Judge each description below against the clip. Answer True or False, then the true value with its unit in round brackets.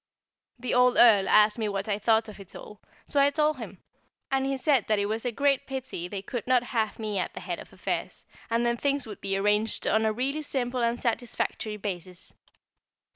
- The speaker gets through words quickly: True (215 wpm)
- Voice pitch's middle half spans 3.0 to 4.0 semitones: True (3.6 semitones)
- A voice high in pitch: True (225 Hz)